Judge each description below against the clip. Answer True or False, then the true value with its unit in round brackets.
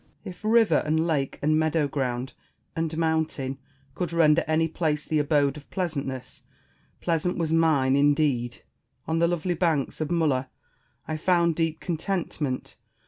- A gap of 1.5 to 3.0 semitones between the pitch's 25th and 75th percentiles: True (2.7 semitones)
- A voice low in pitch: False (155 Hz)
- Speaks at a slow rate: False (145 wpm)